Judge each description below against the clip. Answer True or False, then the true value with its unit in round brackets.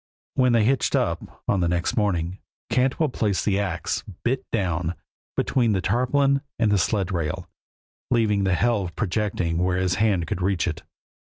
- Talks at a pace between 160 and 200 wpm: True (165 wpm)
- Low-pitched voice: True (100 Hz)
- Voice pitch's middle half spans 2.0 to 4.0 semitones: False (4.5 semitones)